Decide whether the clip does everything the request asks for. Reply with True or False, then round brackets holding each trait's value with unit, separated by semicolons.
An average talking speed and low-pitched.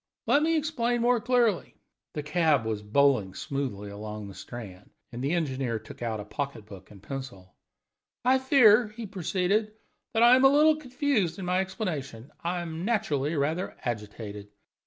False (165 wpm; 155 Hz)